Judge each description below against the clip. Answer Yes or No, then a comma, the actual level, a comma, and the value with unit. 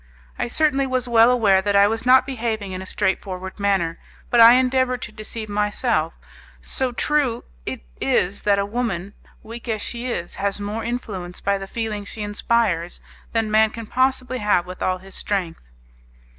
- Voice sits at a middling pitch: No, high, 215 Hz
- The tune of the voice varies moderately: Yes, average, 3.6 semitones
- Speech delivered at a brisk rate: No, average, 175 wpm